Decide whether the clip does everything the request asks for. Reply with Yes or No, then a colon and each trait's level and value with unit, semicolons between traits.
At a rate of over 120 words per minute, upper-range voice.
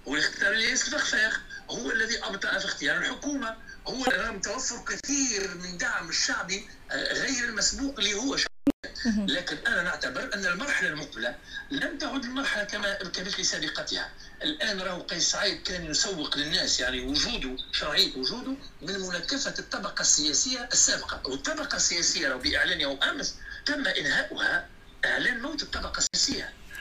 Yes: fast, 135 wpm; high, 240 Hz